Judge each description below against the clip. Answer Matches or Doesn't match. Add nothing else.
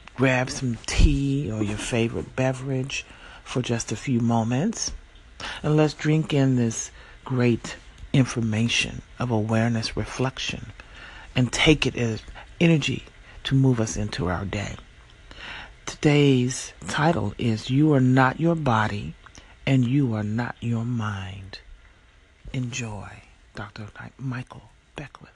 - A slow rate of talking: Matches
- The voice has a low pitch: Matches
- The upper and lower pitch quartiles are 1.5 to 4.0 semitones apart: Matches